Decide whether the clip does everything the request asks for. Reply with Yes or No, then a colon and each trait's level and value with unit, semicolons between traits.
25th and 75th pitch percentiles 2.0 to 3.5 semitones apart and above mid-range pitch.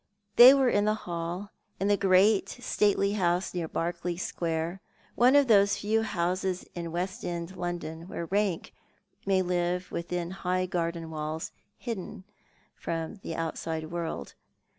No: average, 3.0 semitones; medium, 180 Hz